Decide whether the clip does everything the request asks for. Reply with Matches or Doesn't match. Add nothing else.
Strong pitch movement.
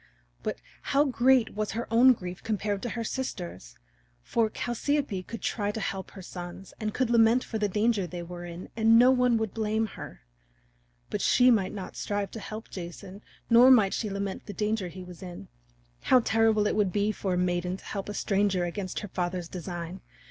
Doesn't match